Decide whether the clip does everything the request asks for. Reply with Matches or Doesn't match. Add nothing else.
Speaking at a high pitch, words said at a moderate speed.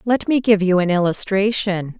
Matches